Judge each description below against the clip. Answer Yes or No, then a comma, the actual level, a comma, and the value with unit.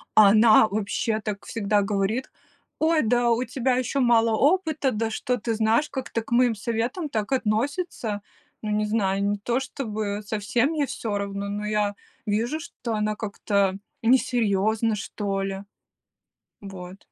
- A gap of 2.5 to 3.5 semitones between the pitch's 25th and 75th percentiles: Yes, average, 3.2 semitones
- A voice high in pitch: Yes, high, 220 Hz